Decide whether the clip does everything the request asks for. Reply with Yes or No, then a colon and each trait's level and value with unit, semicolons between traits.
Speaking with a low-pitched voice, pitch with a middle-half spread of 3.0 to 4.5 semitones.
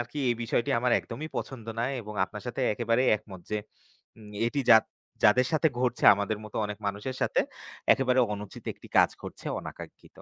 Yes: low, 115 Hz; average, 3.3 semitones